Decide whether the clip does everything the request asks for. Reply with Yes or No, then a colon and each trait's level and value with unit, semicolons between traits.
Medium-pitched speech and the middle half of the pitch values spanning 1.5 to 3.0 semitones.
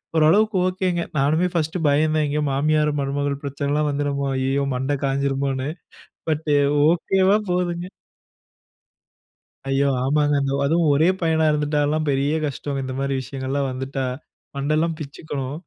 Yes: medium, 145 Hz; narrow, 2.4 semitones